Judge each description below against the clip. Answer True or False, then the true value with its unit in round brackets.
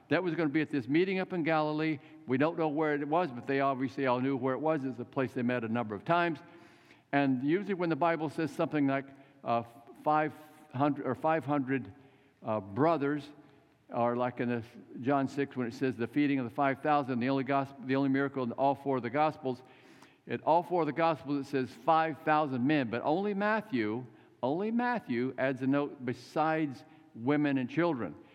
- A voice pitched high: False (140 Hz)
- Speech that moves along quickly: True (210 wpm)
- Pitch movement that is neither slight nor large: True (3.2 semitones)